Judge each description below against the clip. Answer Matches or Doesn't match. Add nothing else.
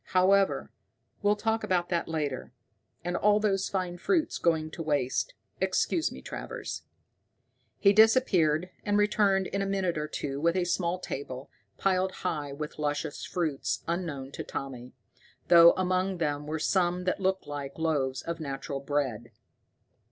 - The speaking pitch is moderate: Matches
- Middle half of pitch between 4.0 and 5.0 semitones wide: Matches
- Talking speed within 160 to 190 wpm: Doesn't match